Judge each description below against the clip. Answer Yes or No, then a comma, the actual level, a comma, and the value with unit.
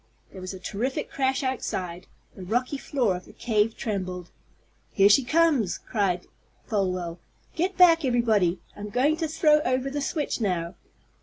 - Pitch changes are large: Yes, wide, 6.8 semitones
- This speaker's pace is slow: No, average, 155 wpm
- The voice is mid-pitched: No, high, 225 Hz